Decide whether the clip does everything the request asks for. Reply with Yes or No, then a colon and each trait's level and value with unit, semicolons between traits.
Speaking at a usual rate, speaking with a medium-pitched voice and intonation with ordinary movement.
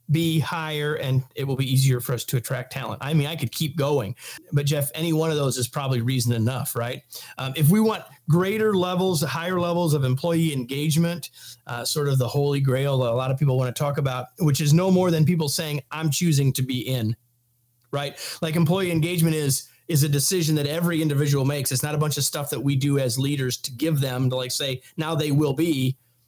No: fast, 230 wpm; medium, 145 Hz; average, 3.6 semitones